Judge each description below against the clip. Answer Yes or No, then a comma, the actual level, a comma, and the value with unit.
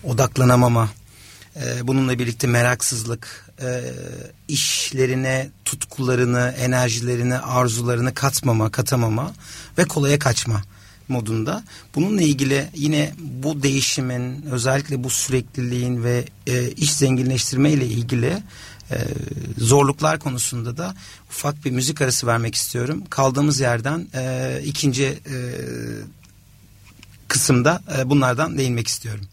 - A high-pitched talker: No, low, 130 Hz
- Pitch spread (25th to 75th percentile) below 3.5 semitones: Yes, average, 2.8 semitones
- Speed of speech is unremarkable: No, slow, 90 wpm